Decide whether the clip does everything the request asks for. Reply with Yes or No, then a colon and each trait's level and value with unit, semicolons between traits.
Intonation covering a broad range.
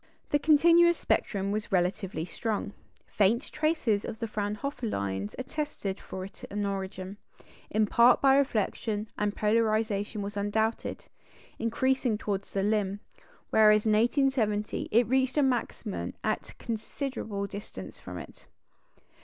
No: average, 3.6 semitones